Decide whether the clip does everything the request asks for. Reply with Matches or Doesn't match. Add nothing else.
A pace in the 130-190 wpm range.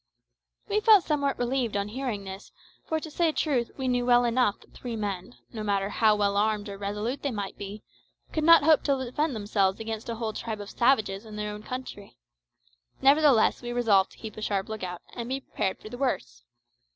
Doesn't match